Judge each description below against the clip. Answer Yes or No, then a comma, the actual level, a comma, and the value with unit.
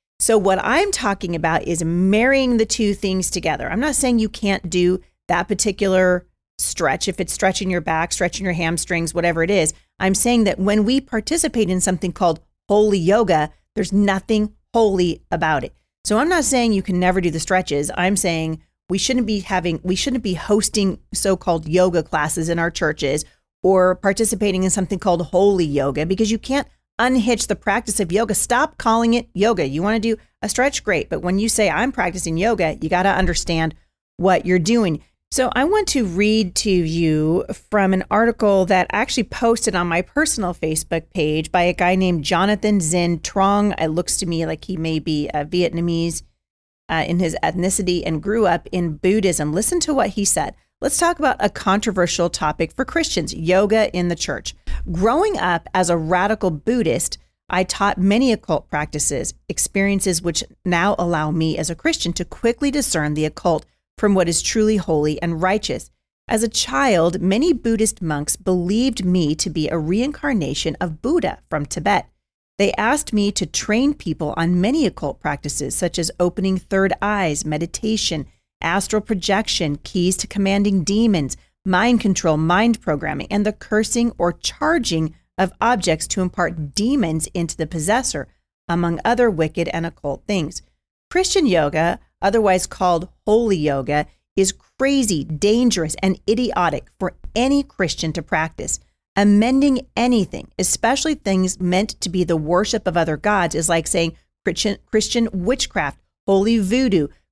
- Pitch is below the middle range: No, high, 190 Hz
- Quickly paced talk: No, average, 170 wpm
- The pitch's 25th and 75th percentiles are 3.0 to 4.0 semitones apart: No, average, 4.4 semitones